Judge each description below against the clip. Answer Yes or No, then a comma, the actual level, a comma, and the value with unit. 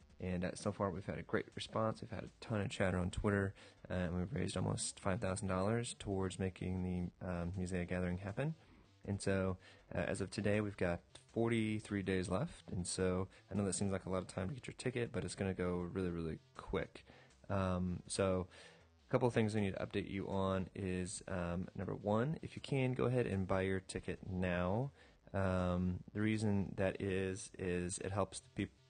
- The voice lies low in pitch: Yes, very low, 95 Hz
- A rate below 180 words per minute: No, fast, 205 wpm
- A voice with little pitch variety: Yes, narrow, 2.3 semitones